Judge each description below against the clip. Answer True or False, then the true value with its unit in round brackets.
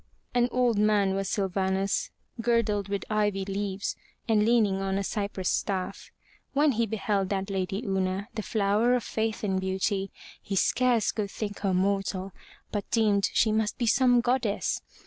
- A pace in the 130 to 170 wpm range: True (160 wpm)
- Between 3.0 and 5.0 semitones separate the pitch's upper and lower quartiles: False (2.4 semitones)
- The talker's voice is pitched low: False (205 Hz)